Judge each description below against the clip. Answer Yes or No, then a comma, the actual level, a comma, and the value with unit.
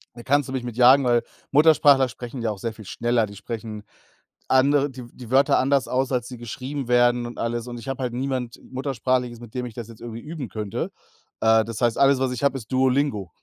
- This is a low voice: Yes, low, 125 Hz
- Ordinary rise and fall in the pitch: No, narrow, 2.3 semitones